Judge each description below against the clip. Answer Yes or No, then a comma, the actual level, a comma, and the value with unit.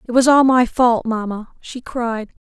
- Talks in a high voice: Yes, high, 240 Hz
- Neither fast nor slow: Yes, average, 195 wpm